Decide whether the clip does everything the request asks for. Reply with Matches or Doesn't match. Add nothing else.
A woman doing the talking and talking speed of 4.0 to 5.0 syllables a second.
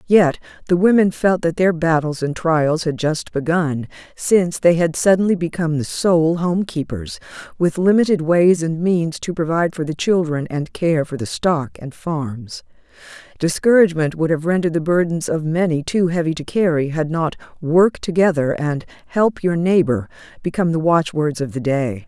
Matches